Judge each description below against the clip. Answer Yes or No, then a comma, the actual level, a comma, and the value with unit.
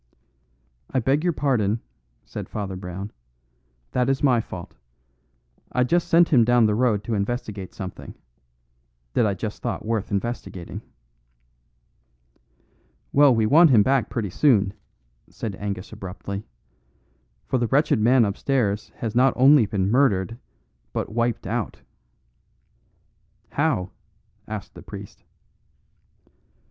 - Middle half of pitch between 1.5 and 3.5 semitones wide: No, average, 4.4 semitones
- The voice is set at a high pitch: No, low, 115 Hz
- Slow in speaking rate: Yes, slow, 120 wpm